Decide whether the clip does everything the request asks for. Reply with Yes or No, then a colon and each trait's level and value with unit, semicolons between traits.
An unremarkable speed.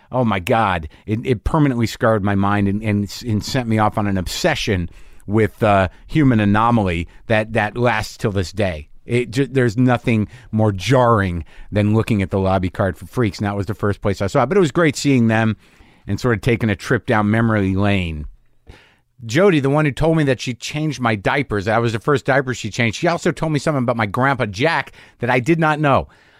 No: fast, 225 wpm